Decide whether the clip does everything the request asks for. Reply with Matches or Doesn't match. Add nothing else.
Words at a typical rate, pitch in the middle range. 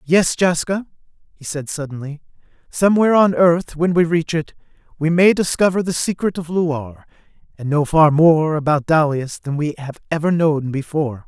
Matches